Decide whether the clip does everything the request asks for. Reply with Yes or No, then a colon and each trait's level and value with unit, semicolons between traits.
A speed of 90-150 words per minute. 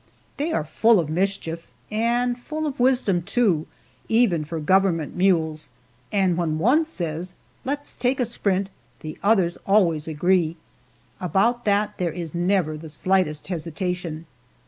Yes: average, 140 wpm